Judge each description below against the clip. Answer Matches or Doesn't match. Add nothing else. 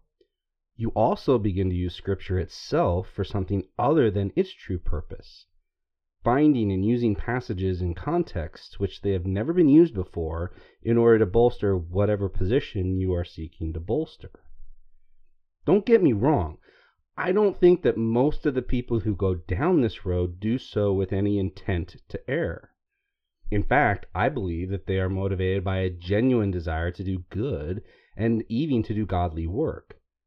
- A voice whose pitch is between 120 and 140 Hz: Doesn't match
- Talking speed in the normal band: Matches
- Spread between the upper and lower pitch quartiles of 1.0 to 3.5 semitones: Doesn't match